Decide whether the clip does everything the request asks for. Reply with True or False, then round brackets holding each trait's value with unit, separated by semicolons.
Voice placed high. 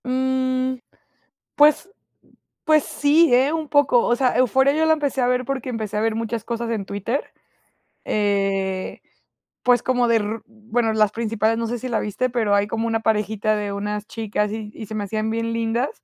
True (230 Hz)